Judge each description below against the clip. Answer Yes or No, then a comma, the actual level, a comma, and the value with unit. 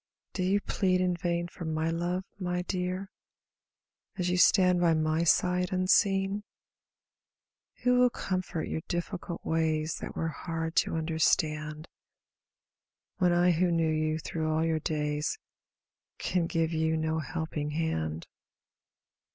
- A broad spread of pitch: No, narrow, 2.4 semitones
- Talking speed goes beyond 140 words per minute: No, slow, 135 wpm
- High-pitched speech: No, medium, 165 Hz